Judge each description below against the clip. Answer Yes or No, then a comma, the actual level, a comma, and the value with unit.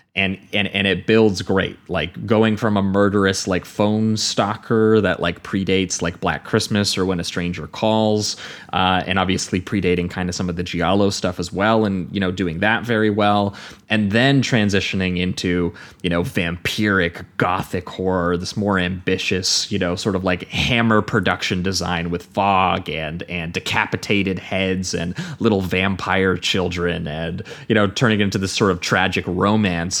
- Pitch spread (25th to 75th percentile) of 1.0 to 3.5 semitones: Yes, average, 2.8 semitones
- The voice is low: Yes, very low, 95 Hz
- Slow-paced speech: No, average, 170 wpm